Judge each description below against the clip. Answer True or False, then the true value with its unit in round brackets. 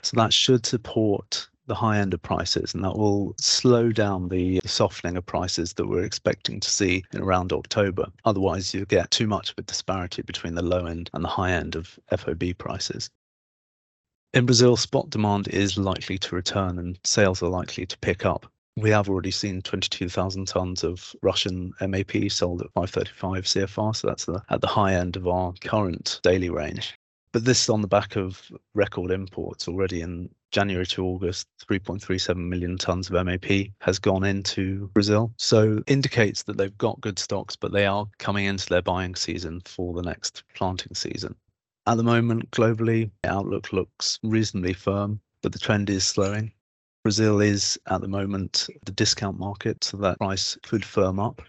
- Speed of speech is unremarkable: True (180 wpm)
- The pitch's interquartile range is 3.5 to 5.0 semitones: False (2.7 semitones)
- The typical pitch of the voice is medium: False (95 Hz)